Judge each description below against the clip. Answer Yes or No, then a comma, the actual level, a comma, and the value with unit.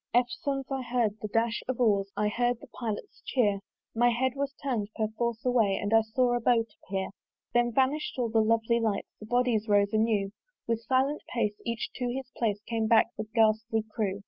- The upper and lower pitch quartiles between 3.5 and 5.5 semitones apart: No, narrow, 2.4 semitones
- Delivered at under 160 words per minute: No, average, 195 wpm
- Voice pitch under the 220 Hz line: No, high, 230 Hz